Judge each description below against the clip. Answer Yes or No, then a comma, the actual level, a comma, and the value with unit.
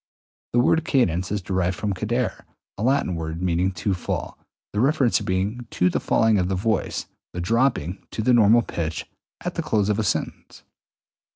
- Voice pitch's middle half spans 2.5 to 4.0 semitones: No, average, 4.6 semitones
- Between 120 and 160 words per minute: No, average, 185 wpm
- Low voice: Yes, low, 105 Hz